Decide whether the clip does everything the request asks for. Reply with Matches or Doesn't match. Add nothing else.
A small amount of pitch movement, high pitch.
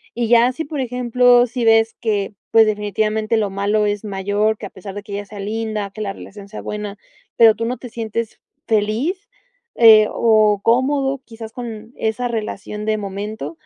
Matches